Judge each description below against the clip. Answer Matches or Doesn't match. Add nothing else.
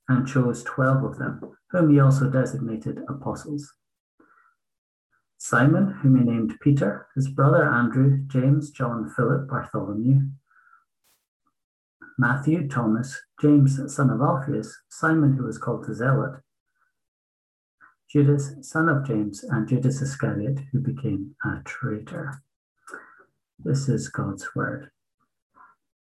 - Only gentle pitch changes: Doesn't match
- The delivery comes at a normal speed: Doesn't match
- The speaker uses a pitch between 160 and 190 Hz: Doesn't match